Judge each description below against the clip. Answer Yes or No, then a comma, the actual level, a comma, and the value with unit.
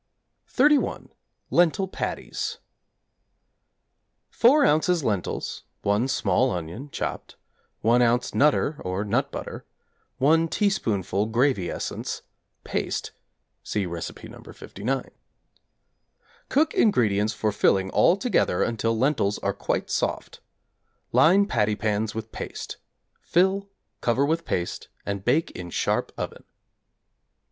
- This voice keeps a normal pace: No, slow, 110 wpm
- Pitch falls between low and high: No, low, 120 Hz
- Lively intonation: Yes, wide, 7.9 semitones